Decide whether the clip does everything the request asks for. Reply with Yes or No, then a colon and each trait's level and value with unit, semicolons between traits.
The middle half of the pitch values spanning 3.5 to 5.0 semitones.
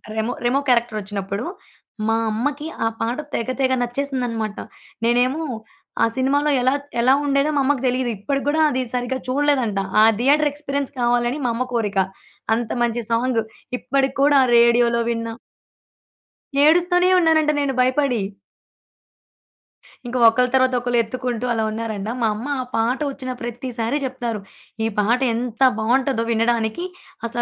No: average, 3.0 semitones